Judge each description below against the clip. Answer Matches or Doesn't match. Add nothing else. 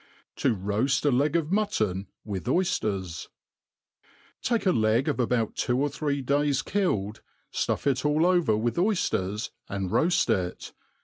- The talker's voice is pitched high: Doesn't match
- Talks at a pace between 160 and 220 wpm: Doesn't match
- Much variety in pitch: Matches